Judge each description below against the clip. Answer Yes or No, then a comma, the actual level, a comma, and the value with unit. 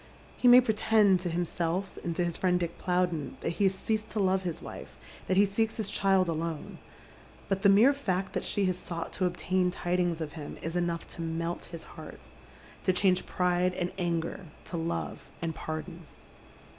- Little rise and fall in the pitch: Yes, narrow, 2.3 semitones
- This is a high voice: No, medium, 180 Hz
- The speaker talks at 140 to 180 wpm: No, average, 195 wpm